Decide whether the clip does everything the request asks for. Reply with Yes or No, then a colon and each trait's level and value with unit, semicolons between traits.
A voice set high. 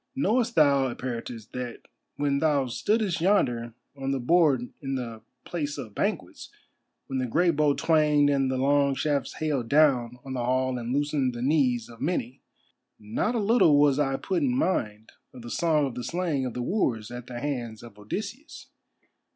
No: low, 135 Hz